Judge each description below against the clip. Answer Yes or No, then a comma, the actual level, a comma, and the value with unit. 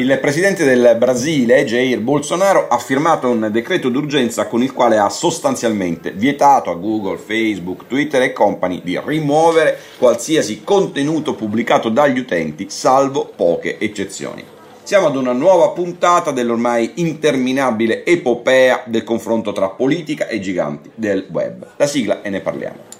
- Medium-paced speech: Yes, average, 140 wpm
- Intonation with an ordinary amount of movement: No, wide, 5.9 semitones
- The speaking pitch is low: Yes, low, 125 Hz